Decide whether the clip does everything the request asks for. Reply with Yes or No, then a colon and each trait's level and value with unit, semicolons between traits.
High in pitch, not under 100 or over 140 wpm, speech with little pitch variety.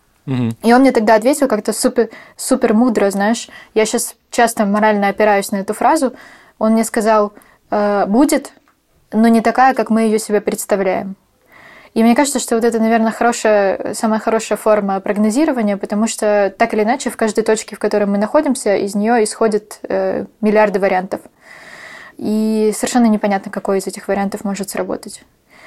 No: high, 220 Hz; fast, 160 wpm; narrow, 2.2 semitones